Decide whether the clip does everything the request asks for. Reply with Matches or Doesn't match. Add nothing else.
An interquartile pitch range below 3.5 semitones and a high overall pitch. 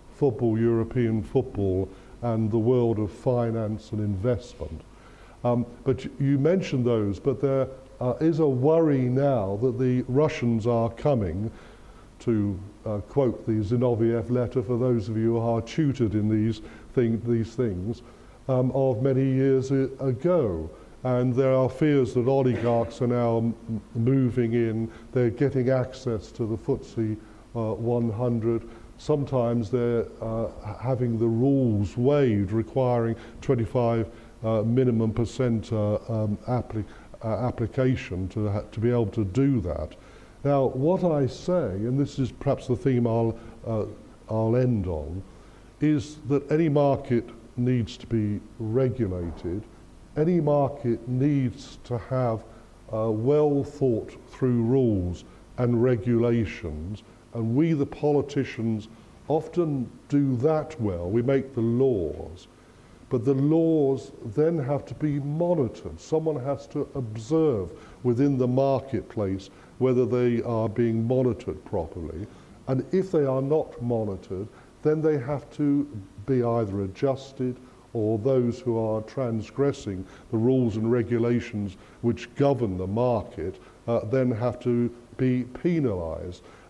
Doesn't match